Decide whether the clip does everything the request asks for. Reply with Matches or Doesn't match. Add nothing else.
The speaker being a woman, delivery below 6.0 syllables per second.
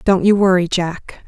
Matches